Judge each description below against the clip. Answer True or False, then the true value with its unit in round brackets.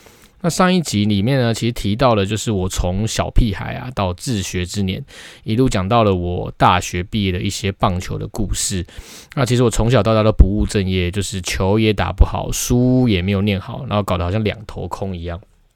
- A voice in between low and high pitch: False (105 Hz)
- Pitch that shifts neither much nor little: True (3.8 semitones)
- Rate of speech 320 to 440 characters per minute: False (305 characters per minute)